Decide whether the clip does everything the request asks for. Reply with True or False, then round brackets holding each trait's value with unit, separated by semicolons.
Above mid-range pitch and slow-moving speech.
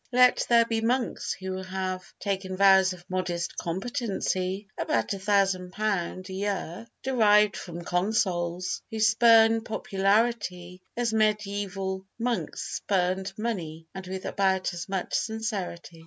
True (195 Hz; 115 wpm)